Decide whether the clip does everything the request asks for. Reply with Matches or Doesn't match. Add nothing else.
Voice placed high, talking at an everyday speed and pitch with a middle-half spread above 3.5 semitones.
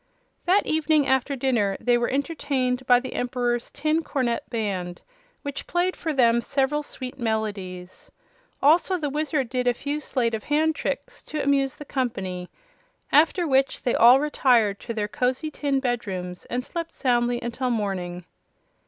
Matches